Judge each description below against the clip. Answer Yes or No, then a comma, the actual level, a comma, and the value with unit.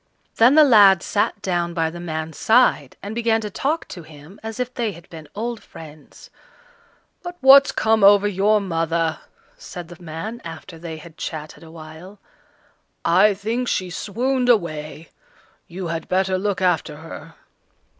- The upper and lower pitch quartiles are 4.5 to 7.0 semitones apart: Yes, average, 5.1 semitones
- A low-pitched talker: No, medium, 185 Hz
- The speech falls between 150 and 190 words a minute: Yes, average, 160 wpm